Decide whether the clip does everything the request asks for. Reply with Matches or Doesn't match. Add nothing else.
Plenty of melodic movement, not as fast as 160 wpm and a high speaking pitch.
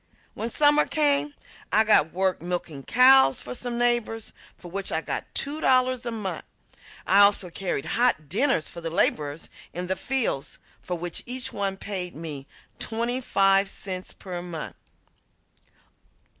Matches